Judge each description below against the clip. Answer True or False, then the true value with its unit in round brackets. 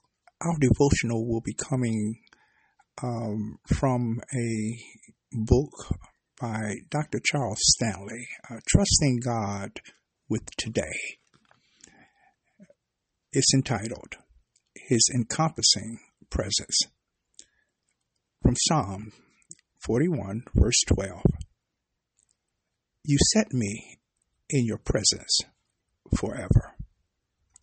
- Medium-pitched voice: False (115 Hz)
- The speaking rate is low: True (75 wpm)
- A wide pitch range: False (3.6 semitones)